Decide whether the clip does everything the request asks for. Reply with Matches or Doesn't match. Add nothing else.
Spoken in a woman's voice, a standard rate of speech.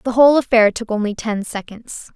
Matches